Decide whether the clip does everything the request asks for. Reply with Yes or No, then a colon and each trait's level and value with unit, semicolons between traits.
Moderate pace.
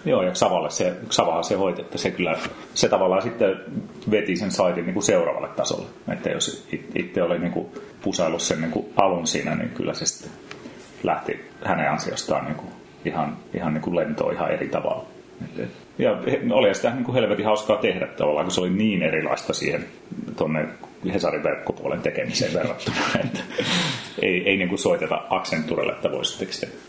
No: fast, 175 wpm